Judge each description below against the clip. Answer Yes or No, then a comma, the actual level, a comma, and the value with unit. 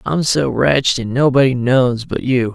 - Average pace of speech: Yes, average, 190 wpm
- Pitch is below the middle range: Yes, low, 130 Hz